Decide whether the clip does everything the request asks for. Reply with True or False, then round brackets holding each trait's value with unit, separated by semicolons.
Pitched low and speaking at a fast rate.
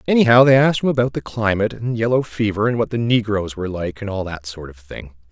True (105 Hz; 250 wpm)